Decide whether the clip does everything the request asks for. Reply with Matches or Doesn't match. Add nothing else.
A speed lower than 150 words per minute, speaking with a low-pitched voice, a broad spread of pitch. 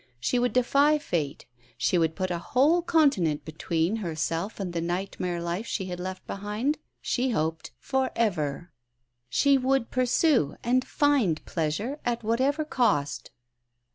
Doesn't match